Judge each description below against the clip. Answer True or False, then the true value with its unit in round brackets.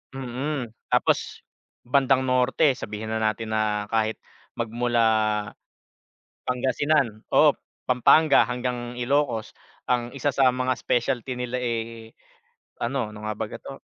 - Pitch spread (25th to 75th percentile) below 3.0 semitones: True (2.6 semitones)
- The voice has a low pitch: True (120 Hz)